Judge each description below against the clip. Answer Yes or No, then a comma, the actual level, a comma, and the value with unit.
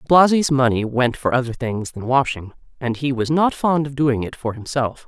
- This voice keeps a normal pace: No, fast, 215 wpm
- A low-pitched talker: Yes, low, 130 Hz